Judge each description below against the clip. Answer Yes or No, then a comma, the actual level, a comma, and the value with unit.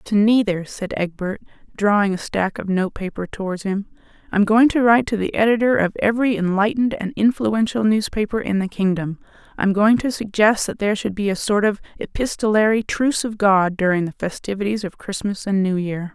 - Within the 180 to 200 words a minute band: Yes, average, 185 wpm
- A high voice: Yes, high, 205 Hz